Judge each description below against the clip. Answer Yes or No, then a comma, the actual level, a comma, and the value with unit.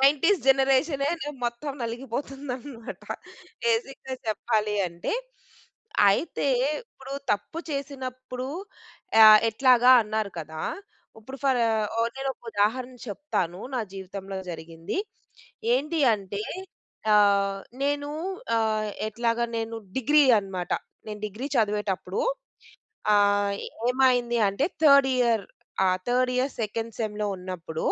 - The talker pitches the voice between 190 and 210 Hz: No, high, 230 Hz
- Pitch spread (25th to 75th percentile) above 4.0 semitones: Yes, average, 4.7 semitones